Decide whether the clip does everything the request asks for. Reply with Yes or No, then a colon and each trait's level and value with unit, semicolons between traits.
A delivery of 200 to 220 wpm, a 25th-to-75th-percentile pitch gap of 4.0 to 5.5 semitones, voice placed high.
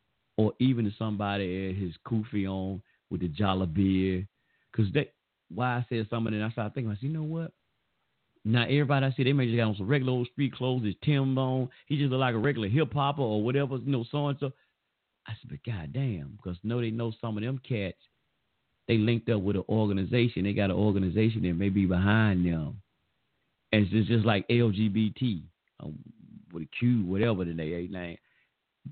No: fast, 205 wpm; average, 4.5 semitones; low, 110 Hz